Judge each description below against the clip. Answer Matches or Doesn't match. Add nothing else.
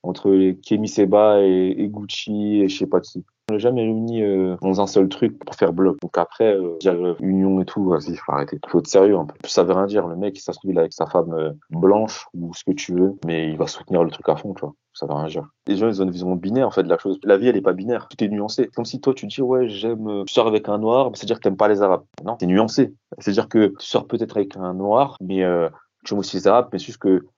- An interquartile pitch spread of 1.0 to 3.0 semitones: Matches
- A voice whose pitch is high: Doesn't match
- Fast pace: Matches